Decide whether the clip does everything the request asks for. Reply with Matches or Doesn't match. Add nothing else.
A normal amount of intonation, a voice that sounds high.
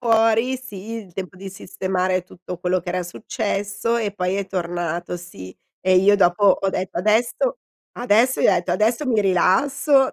Matches